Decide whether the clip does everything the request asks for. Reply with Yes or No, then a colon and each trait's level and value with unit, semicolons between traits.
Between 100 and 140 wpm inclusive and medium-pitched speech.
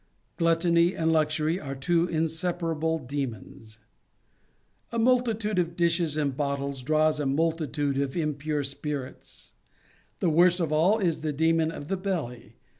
Yes: slow, 135 wpm; medium, 160 Hz